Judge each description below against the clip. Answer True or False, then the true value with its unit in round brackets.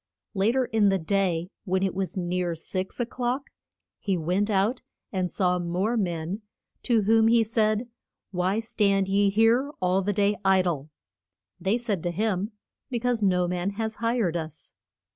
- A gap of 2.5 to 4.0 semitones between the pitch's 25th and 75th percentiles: True (3.6 semitones)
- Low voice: False (195 Hz)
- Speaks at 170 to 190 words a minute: False (160 wpm)